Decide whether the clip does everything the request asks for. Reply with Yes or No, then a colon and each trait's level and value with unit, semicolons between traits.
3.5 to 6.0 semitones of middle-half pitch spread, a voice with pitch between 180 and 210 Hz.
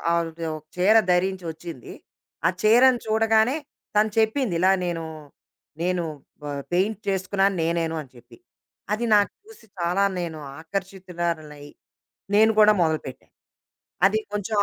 Yes: average, 4.2 semitones; high, 190 Hz